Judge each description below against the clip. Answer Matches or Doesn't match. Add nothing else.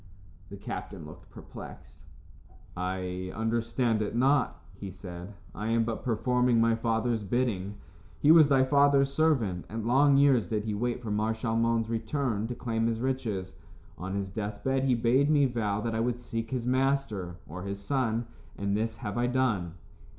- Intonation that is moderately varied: Matches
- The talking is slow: Doesn't match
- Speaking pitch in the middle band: Doesn't match